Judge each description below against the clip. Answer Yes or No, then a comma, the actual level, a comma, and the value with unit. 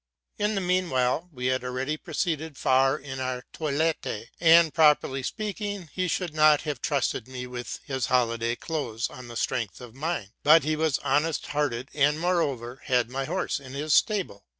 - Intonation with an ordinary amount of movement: Yes, average, 4.2 semitones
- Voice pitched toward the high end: No, medium, 145 Hz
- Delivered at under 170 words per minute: No, average, 180 wpm